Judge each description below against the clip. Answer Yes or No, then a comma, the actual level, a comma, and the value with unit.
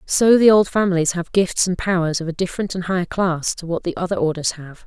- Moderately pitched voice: Yes, medium, 180 Hz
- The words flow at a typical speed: No, fast, 245 wpm